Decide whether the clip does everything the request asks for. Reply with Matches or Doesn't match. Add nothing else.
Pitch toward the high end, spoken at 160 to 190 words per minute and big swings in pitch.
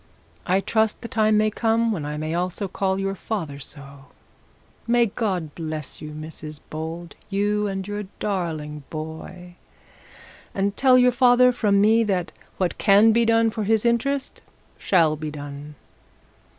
Doesn't match